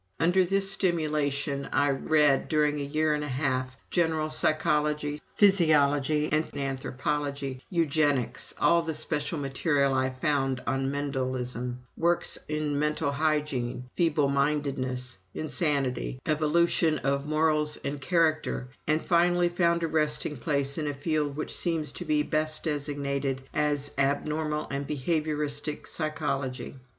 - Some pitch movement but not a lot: No, narrow, 2.0 semitones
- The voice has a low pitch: No, medium, 150 Hz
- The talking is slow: Yes, slow, 125 wpm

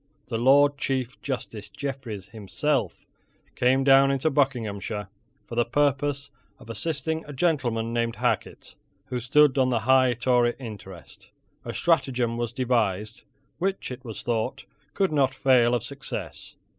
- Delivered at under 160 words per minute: Yes, average, 140 wpm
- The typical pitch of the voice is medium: No, low, 125 Hz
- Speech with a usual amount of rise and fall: Yes, average, 3.1 semitones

